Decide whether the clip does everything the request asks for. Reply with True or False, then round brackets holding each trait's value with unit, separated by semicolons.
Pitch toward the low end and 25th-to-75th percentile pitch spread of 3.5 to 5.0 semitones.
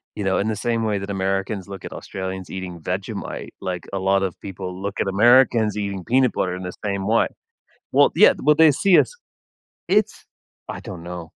False (100 Hz; 2.5 semitones)